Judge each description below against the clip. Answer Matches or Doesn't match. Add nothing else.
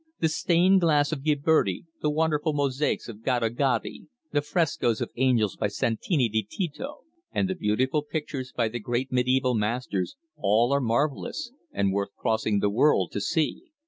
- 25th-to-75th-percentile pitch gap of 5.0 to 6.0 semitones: Matches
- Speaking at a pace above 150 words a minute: Matches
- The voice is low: Matches